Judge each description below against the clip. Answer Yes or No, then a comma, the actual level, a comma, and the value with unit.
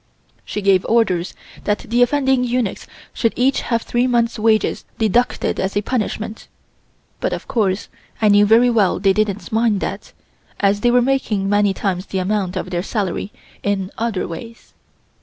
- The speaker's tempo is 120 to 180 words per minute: Yes, average, 165 wpm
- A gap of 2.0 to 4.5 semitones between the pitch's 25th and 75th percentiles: Yes, average, 3.2 semitones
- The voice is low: No, high, 215 Hz